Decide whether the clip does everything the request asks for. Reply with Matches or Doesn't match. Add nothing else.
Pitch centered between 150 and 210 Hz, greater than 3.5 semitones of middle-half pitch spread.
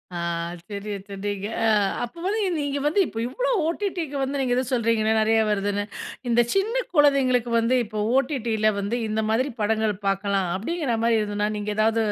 Doesn't match